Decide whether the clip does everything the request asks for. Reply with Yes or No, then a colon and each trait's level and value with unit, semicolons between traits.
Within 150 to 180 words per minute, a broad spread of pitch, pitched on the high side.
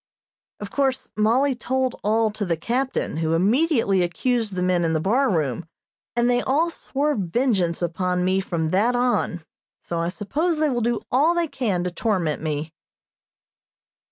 Yes: average, 165 wpm; wide, 6.8 semitones; high, 215 Hz